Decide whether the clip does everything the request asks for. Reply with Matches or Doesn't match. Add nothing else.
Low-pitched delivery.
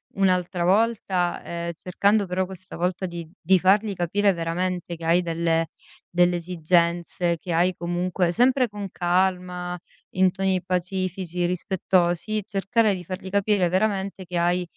Doesn't match